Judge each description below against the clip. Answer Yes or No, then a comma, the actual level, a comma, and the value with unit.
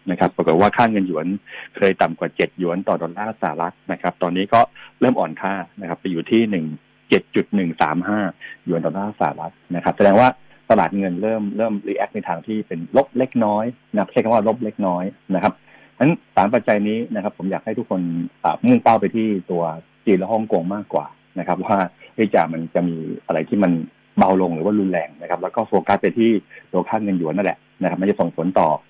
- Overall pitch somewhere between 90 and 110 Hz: Yes, low, 100 Hz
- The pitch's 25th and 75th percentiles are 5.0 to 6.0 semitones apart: No, average, 4.1 semitones